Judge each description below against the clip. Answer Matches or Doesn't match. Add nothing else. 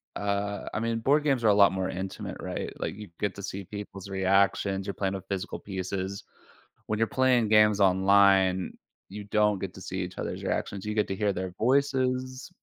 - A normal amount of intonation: Doesn't match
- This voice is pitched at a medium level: Doesn't match